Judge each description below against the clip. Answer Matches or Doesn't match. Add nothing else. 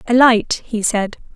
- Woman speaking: Matches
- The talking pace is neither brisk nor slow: Matches